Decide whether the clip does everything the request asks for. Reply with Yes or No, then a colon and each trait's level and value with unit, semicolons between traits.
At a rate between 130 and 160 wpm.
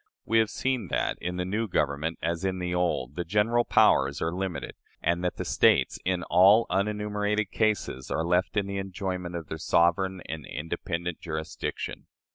No: average, 175 wpm